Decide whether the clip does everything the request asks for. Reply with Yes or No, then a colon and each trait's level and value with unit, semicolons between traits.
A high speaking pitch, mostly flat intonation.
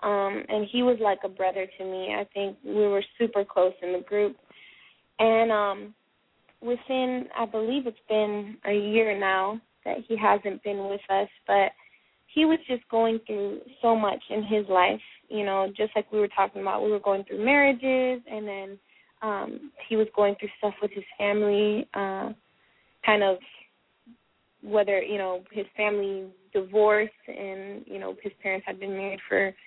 Yes: high, 205 Hz; narrow, 2.0 semitones